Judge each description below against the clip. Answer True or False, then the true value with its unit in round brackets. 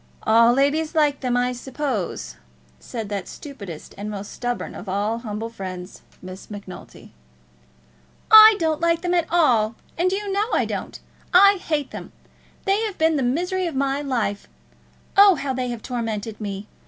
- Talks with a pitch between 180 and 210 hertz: False (255 Hz)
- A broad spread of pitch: True (7.6 semitones)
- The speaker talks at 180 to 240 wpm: False (165 wpm)